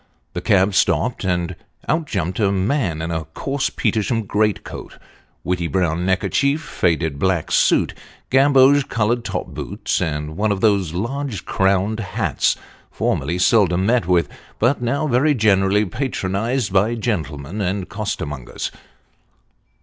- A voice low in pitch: Yes, low, 100 Hz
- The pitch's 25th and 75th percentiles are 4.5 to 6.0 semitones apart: Yes, average, 4.9 semitones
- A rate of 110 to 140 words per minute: Yes, slow, 135 wpm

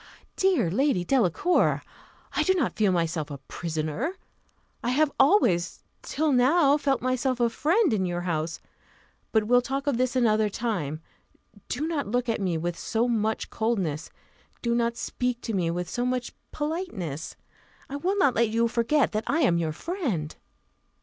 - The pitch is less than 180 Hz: No, high, 235 Hz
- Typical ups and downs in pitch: No, wide, 7.6 semitones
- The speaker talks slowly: No, average, 165 wpm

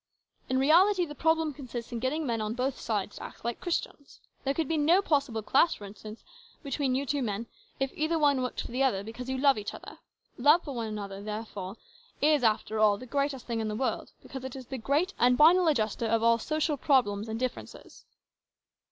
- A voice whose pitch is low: No, very high, 260 Hz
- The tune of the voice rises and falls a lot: No, average, 4.7 semitones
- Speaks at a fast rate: Yes, fast, 215 wpm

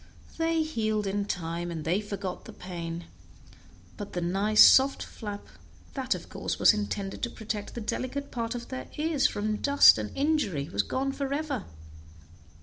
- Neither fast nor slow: Yes, average, 160 wpm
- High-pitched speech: Yes, high, 215 Hz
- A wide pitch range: Yes, wide, 6.3 semitones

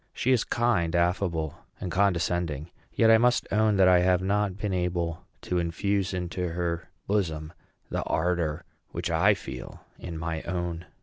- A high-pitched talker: No, very low, 90 Hz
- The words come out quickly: No, average, 160 wpm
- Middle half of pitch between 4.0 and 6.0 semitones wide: No, average, 2.9 semitones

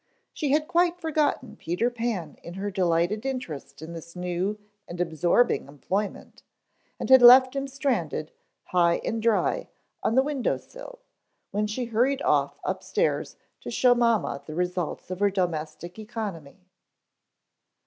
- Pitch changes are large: Yes, wide, 6.7 semitones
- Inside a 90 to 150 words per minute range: Yes, average, 145 wpm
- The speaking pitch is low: No, high, 210 Hz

